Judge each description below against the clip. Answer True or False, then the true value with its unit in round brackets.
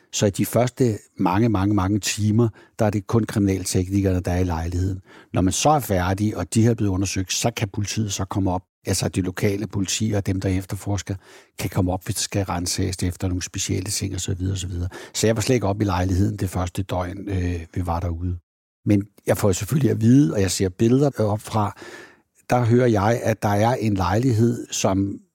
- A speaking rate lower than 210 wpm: False (220 wpm)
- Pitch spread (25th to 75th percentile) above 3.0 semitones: False (2.7 semitones)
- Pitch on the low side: True (100 Hz)